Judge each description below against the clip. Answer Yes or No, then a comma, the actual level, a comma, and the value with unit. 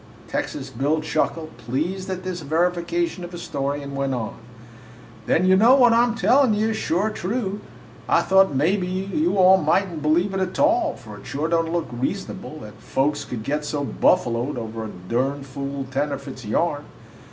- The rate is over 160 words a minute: Yes, average, 180 wpm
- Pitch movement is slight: No, wide, 5.5 semitones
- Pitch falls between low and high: Yes, medium, 160 Hz